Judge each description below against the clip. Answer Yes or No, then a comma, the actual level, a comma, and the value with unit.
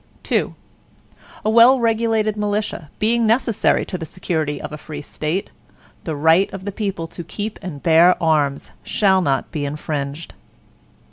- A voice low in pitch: No, medium, 180 Hz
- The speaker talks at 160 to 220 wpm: No, average, 150 wpm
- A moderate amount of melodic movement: No, wide, 5.7 semitones